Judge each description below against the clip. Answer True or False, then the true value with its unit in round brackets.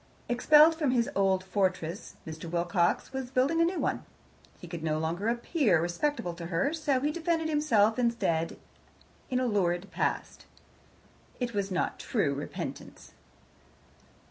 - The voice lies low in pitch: False (210 Hz)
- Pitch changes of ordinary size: False (8.2 semitones)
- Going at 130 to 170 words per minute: True (145 wpm)